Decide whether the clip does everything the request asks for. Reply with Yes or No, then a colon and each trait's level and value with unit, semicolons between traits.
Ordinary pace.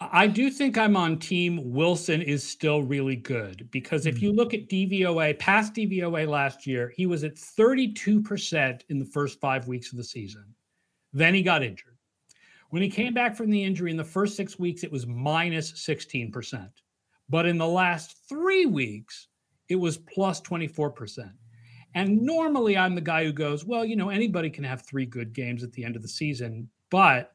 Yes: average, 190 wpm